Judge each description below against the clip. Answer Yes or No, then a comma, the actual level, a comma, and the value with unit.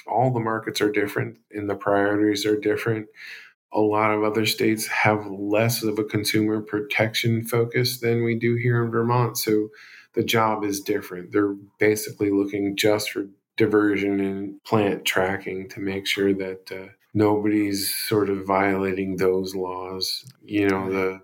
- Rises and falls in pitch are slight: Yes, narrow, 1.9 semitones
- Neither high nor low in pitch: No, low, 105 Hz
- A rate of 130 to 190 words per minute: Yes, average, 160 wpm